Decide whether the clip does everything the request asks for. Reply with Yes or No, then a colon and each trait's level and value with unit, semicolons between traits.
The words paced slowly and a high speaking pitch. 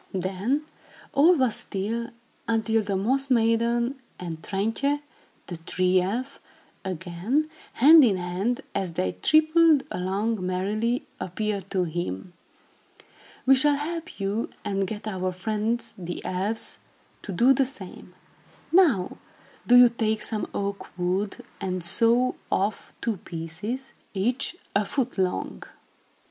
Yes: slow, 125 wpm; high, 215 Hz